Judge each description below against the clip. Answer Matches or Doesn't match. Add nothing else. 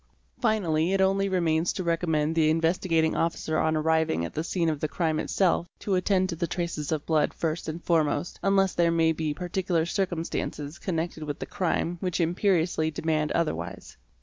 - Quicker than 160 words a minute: Matches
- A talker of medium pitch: Matches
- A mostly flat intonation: Matches